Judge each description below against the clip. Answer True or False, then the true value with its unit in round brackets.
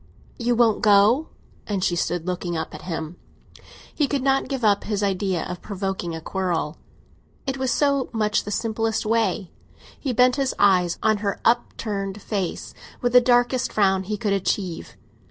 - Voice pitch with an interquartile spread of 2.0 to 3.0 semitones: False (4.3 semitones)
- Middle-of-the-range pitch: False (210 Hz)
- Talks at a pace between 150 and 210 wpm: True (170 wpm)